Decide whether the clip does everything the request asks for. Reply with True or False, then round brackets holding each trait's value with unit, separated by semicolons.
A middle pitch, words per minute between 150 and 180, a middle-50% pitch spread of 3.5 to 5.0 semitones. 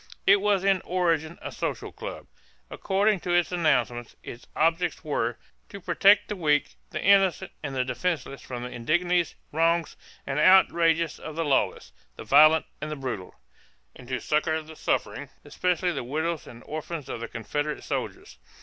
True (160 Hz; 165 wpm; 4.4 semitones)